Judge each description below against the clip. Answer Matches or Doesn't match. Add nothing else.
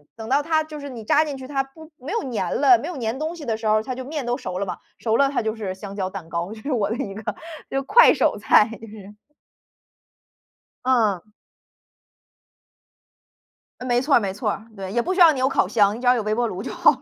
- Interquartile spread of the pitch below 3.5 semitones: Doesn't match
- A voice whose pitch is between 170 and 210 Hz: Doesn't match